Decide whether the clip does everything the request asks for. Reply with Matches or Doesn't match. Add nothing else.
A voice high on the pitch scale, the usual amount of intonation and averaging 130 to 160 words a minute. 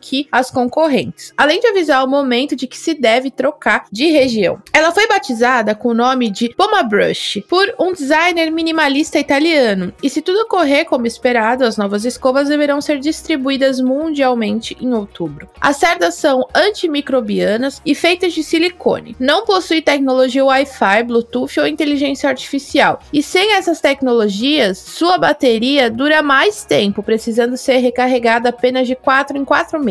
Matches